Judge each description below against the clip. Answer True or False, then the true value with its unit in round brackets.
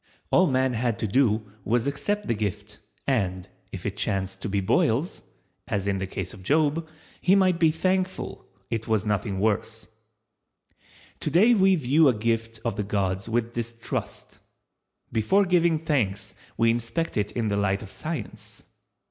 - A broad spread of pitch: True (7.0 semitones)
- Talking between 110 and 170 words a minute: True (165 wpm)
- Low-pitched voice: True (115 Hz)